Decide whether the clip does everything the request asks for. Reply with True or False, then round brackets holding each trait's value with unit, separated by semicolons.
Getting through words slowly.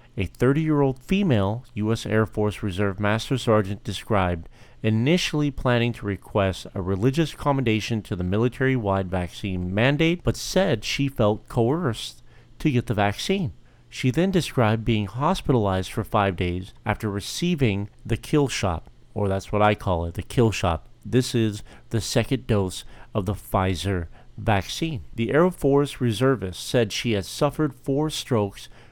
False (155 wpm)